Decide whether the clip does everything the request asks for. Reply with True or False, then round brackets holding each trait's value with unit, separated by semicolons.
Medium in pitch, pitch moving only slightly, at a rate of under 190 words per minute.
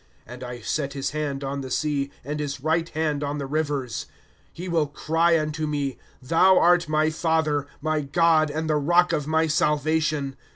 False (150 Hz; 2.1 semitones; 195 wpm)